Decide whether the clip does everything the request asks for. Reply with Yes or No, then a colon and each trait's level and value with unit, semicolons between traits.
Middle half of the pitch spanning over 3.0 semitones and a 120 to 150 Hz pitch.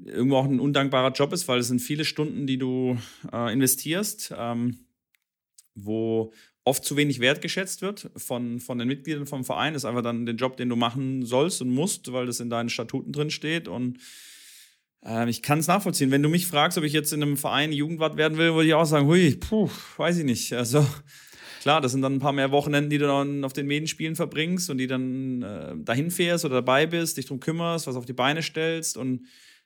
Yes: average, 3.6 semitones; medium, 140 Hz